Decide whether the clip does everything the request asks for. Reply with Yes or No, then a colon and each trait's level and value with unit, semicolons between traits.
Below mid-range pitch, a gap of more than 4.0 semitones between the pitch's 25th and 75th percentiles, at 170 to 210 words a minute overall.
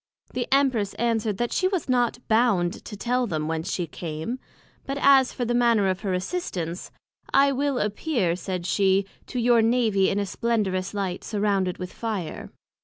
No: high, 210 Hz; average, 4.7 semitones; average, 175 wpm